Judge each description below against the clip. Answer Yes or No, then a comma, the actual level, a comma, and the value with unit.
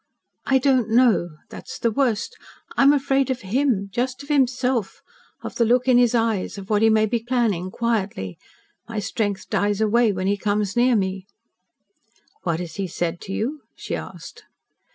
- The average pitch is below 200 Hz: No, high, 225 Hz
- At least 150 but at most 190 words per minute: Yes, average, 180 wpm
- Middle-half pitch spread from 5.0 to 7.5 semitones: No, average, 4.1 semitones